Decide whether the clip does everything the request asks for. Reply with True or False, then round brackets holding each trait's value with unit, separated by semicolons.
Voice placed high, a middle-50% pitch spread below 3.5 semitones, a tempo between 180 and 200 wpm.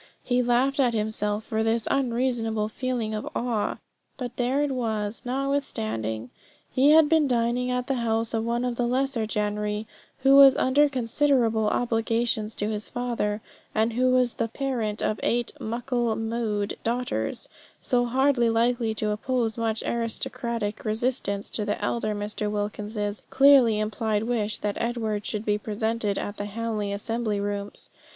False (230 Hz; 2.8 semitones; 155 wpm)